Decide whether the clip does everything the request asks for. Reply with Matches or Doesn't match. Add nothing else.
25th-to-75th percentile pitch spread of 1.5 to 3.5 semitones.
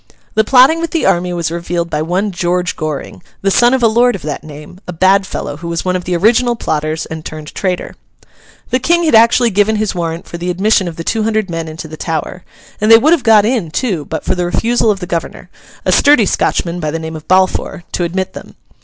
Doesn't match